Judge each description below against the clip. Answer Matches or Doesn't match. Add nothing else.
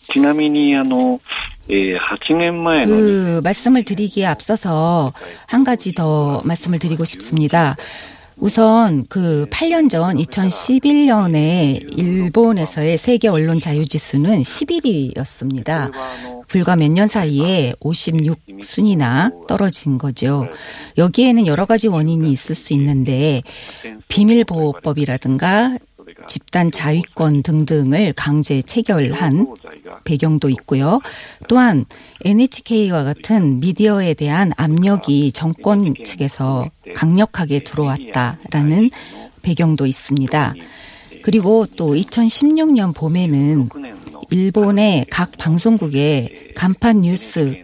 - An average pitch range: Doesn't match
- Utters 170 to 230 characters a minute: Matches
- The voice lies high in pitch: Doesn't match